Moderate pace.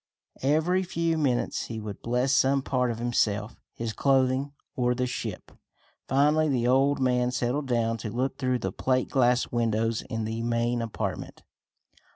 Yes: average, 160 wpm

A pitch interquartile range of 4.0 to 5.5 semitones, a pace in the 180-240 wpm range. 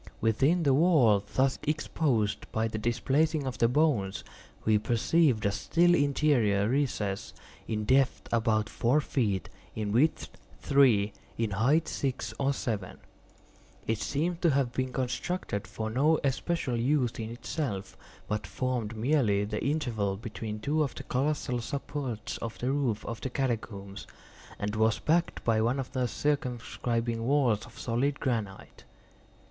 No: average, 4.5 semitones; average, 145 wpm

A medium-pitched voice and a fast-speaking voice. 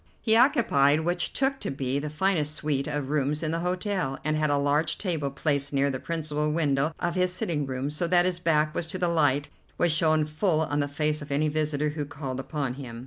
Yes: medium, 150 Hz; fast, 230 wpm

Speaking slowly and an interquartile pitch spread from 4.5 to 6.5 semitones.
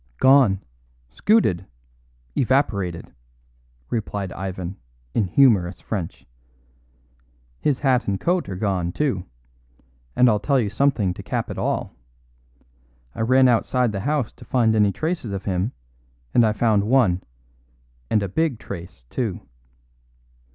Yes: slow, 130 wpm; average, 5.3 semitones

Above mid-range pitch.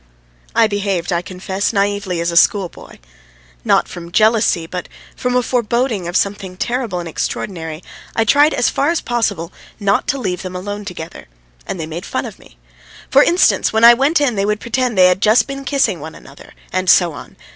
Yes: high, 205 Hz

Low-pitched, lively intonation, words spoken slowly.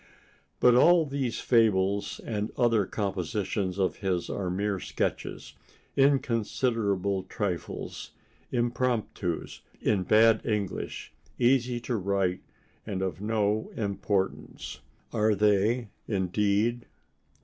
No: low, 105 Hz; average, 3.3 semitones; slow, 95 wpm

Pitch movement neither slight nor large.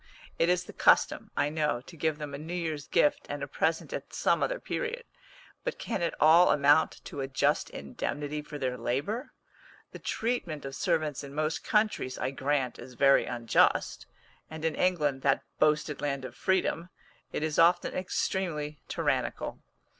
Yes: average, 3.8 semitones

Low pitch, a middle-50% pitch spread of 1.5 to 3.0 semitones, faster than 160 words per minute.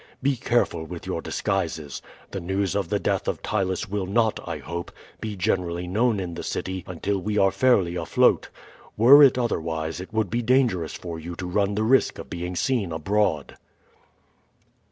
No: very low, 95 Hz; average, 4.2 semitones; average, 175 wpm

